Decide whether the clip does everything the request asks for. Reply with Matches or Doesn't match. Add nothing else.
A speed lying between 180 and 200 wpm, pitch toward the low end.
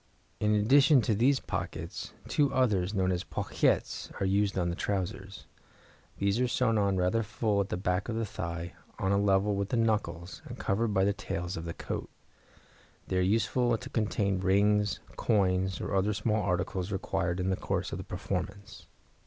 Matches